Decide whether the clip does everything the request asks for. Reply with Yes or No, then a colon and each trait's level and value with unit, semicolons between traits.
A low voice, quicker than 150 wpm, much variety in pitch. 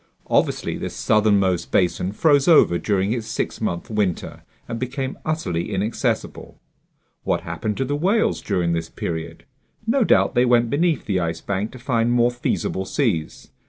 Yes: low, 110 Hz; average, 160 wpm; wide, 5.9 semitones